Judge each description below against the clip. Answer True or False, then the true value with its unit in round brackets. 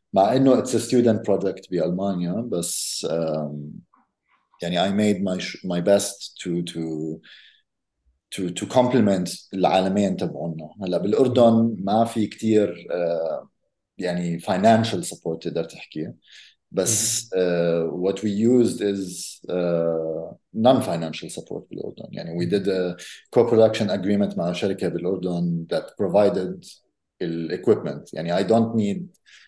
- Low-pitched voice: True (95 Hz)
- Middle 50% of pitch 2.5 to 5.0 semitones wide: True (4.2 semitones)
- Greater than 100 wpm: True (120 wpm)